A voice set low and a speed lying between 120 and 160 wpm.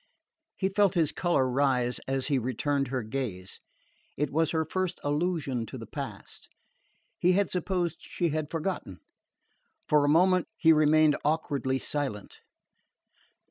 No: medium, 150 Hz; average, 140 wpm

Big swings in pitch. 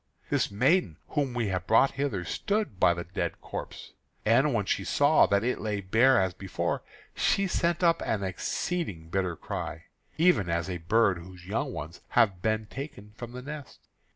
Yes: wide, 6.6 semitones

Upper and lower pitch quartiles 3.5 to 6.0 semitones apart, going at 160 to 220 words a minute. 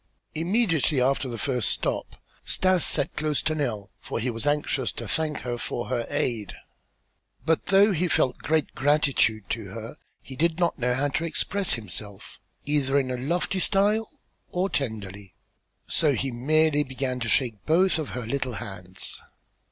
Yes: average, 5.1 semitones; average, 165 wpm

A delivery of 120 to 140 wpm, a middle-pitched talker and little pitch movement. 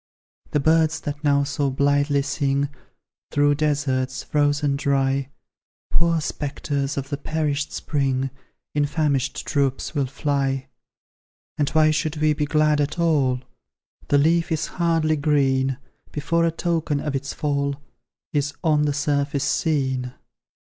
Yes: slow, 135 wpm; medium, 145 Hz; narrow, 1.7 semitones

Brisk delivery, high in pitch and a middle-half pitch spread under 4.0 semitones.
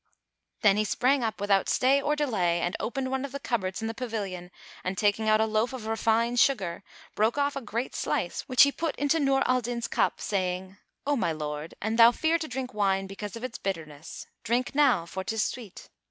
No: fast, 215 wpm; high, 225 Hz; average, 5.0 semitones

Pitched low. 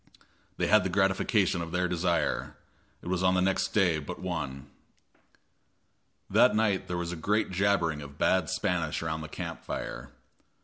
Yes: very low, 90 Hz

